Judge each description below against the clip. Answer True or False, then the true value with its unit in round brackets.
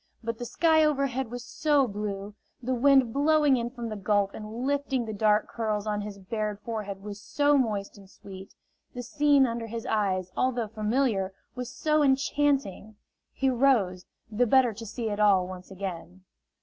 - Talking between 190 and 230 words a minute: False (175 wpm)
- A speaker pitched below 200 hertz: False (225 Hz)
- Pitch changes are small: False (4.5 semitones)